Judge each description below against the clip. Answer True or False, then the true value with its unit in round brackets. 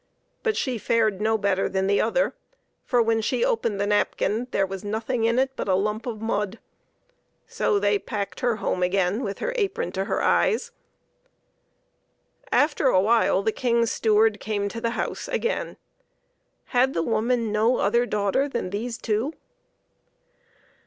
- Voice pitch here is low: False (220 Hz)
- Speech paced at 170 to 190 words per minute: False (160 wpm)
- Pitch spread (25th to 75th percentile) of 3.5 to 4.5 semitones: False (3.1 semitones)